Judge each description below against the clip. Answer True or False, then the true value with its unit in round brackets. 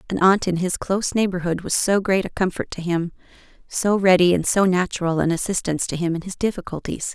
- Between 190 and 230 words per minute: True (200 wpm)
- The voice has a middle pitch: True (180 Hz)